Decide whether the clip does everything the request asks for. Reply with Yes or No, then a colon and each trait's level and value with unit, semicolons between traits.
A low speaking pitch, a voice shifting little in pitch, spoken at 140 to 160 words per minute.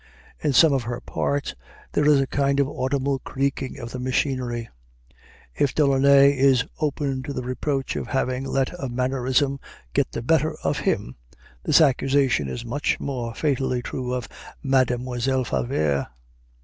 Yes: low, 130 Hz; narrow, 2.0 semitones; average, 150 wpm